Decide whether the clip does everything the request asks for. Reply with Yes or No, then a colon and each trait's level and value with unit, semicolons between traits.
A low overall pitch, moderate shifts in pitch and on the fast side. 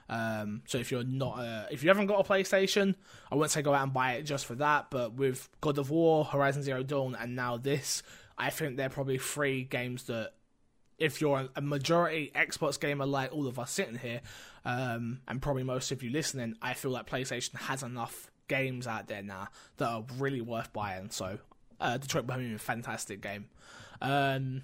Yes: low, 130 Hz; average, 3.2 semitones; fast, 210 wpm